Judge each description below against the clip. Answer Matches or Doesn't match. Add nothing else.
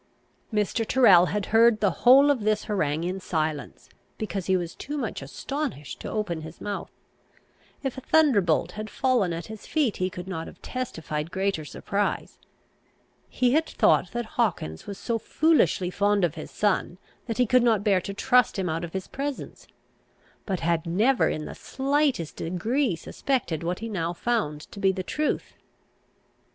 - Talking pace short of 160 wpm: Doesn't match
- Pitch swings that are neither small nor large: Doesn't match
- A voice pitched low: Doesn't match